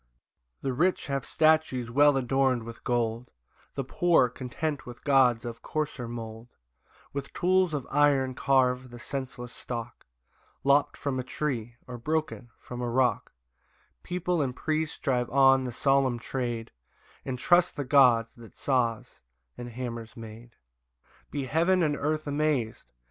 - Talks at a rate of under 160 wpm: Yes, average, 150 wpm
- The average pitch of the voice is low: Yes, low, 130 Hz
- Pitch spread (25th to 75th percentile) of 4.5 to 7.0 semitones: No, average, 3.4 semitones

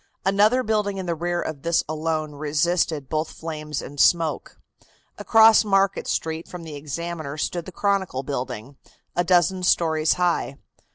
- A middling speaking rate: Yes, average, 150 wpm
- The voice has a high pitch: No, medium, 165 Hz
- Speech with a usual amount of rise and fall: Yes, average, 3.2 semitones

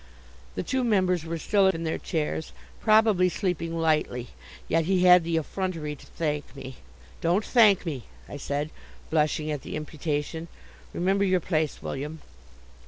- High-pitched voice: No, medium, 165 Hz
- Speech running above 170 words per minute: No, average, 150 wpm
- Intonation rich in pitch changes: No, average, 3.4 semitones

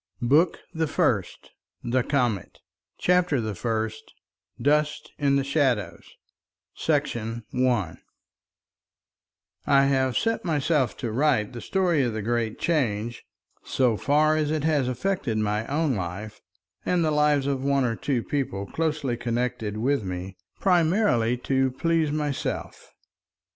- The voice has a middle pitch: No, low, 130 Hz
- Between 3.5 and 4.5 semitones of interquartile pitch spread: No, average, 4.9 semitones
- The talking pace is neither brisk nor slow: No, slow, 130 wpm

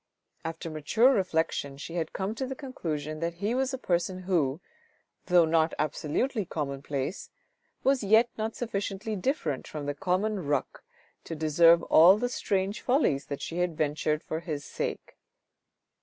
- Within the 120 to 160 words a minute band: Yes, average, 155 wpm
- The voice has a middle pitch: Yes, medium, 170 Hz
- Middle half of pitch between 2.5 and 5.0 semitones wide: No, wide, 5.6 semitones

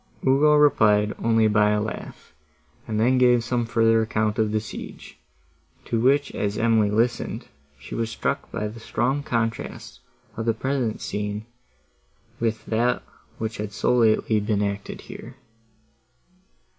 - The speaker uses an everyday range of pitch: No, narrow, 2.1 semitones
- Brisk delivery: No, average, 145 wpm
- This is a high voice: No, low, 115 Hz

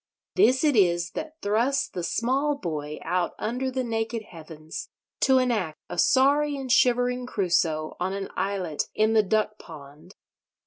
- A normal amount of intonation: No, wide, 6.8 semitones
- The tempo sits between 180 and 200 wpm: No, average, 150 wpm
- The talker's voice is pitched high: Yes, high, 215 Hz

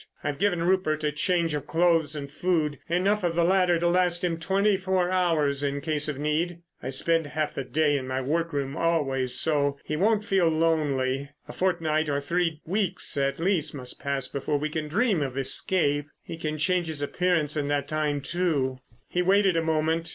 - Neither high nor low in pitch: Yes, medium, 160 Hz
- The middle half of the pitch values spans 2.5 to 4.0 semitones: Yes, average, 3.6 semitones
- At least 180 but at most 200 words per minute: Yes, average, 190 wpm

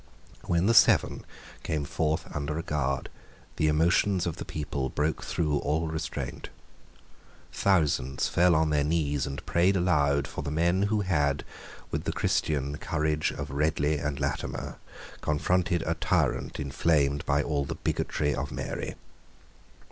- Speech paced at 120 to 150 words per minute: Yes, average, 145 wpm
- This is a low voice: Yes, very low, 75 Hz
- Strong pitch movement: No, average, 2.7 semitones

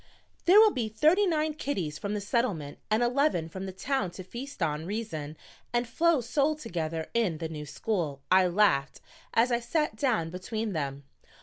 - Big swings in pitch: Yes, wide, 7.8 semitones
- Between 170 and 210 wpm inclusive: Yes, average, 180 wpm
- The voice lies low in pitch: No, high, 215 Hz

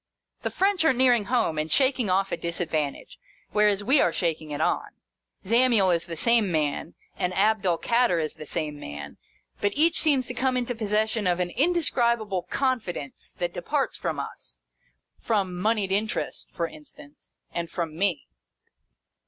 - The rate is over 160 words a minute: Yes, average, 170 wpm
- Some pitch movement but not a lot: No, wide, 6.2 semitones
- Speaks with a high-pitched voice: Yes, high, 200 Hz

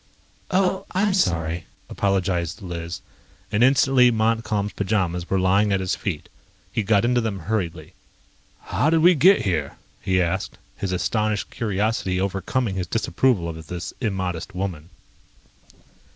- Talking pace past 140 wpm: No, slow, 135 wpm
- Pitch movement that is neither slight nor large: Yes, average, 4.1 semitones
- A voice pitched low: Yes, low, 100 Hz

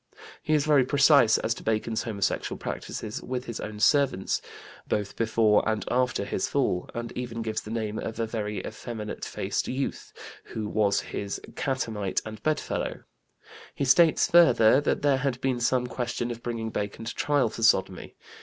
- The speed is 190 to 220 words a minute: No, average, 170 wpm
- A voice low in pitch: Yes, low, 115 Hz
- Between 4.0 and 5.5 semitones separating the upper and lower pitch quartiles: No, average, 3.3 semitones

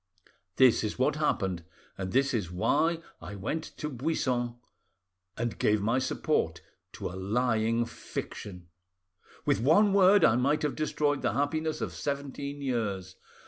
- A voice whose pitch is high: No, low, 130 Hz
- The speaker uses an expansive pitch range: Yes, wide, 5.7 semitones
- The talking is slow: No, average, 145 wpm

